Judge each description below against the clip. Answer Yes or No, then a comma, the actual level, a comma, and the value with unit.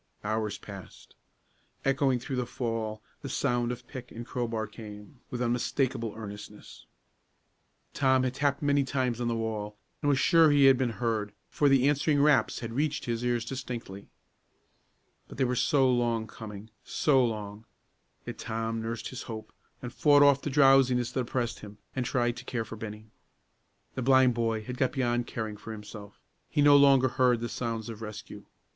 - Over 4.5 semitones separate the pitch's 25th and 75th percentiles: No, average, 3.0 semitones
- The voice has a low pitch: Yes, low, 120 Hz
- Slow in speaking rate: No, average, 175 wpm